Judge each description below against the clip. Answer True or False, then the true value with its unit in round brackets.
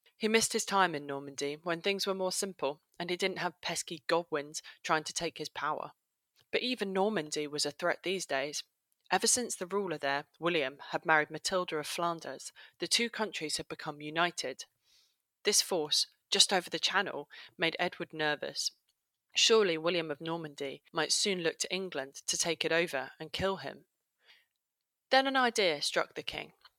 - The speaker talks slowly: False (175 wpm)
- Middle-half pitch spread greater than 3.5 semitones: True (3.9 semitones)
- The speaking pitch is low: False (170 Hz)